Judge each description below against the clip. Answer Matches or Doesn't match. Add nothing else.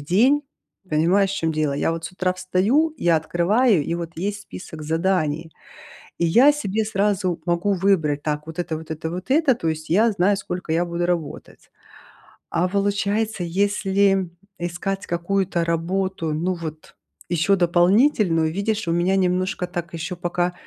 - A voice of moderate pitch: Matches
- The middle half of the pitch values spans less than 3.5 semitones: Matches